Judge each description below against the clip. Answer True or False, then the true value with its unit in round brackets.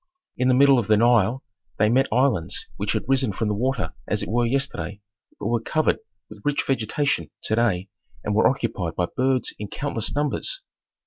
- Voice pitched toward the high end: False (120 Hz)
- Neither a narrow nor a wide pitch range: True (4.1 semitones)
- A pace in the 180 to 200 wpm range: True (190 wpm)